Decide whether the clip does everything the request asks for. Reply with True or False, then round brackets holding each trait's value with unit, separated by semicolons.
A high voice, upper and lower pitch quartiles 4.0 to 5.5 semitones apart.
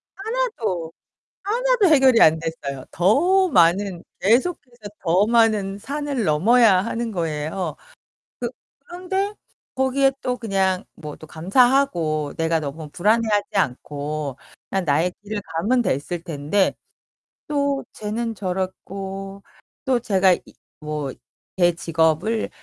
False (195 Hz; 7.2 semitones)